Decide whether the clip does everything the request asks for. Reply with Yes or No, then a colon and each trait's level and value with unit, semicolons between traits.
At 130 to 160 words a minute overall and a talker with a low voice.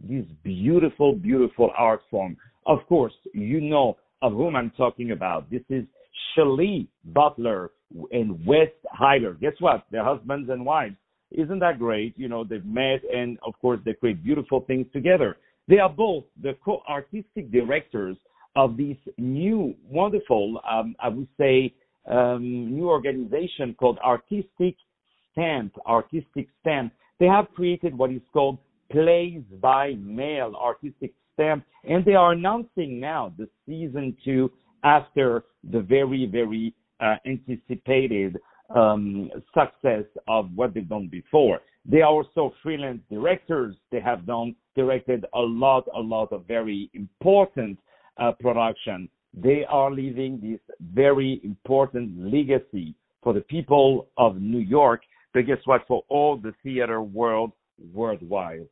Yes: average, 140 wpm; low, 130 Hz